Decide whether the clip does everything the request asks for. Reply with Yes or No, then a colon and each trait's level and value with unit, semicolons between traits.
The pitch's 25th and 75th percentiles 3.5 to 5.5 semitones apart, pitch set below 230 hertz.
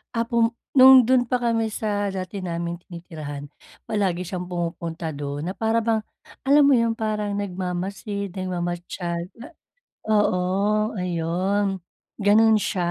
Yes: average, 4.0 semitones; high, 190 Hz